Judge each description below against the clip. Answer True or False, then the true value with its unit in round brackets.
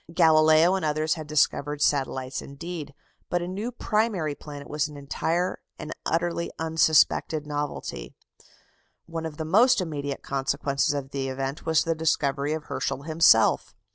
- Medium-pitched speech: True (155 Hz)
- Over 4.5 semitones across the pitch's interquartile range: False (2.7 semitones)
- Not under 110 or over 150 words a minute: True (145 wpm)